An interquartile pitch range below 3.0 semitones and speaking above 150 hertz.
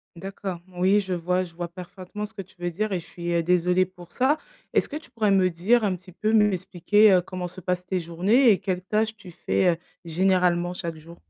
Yes: narrow, 2.6 semitones; medium, 185 Hz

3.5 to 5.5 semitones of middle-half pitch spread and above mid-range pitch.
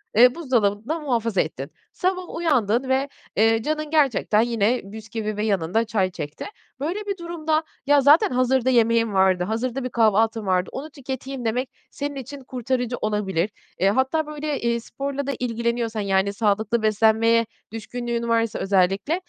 Yes: average, 4.1 semitones; high, 235 Hz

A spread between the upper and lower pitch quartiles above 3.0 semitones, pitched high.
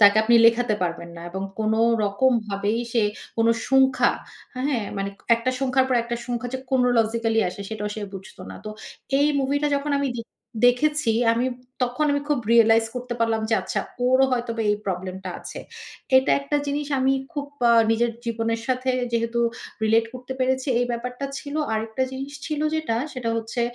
No: average, 2.7 semitones; high, 240 Hz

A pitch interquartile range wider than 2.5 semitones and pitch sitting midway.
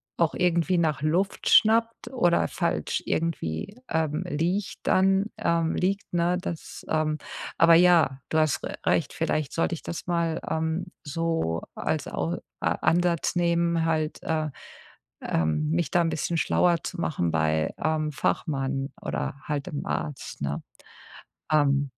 Yes: average, 2.9 semitones; medium, 160 Hz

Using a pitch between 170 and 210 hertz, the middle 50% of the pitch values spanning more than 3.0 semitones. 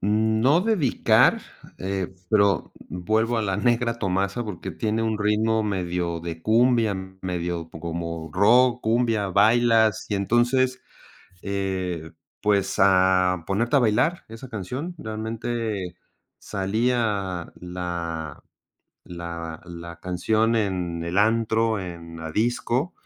No: low, 100 Hz; average, 4.2 semitones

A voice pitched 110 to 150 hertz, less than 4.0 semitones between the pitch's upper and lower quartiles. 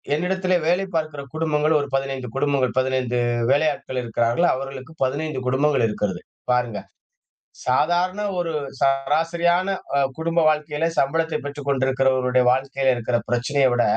Yes: medium, 140 Hz; average, 3.6 semitones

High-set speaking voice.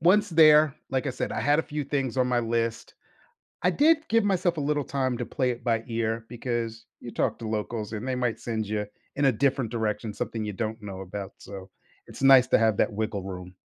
No: low, 120 Hz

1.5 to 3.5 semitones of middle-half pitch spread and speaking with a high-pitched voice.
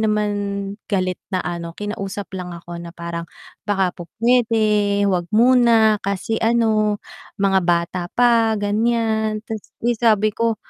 Yes: average, 3.2 semitones; high, 210 Hz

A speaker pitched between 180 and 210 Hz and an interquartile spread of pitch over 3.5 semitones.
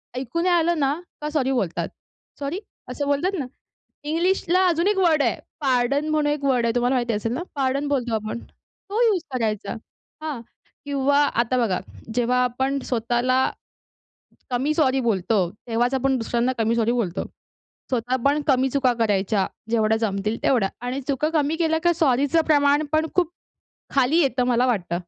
No: very high, 260 Hz; average, 4.2 semitones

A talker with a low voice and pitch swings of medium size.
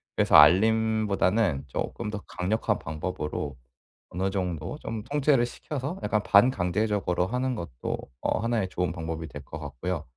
Yes: low, 100 Hz; average, 4.6 semitones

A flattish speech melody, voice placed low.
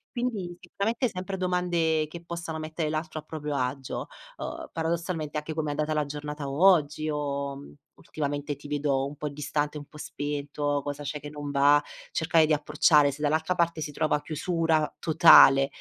No: narrow, 2.1 semitones; medium, 150 Hz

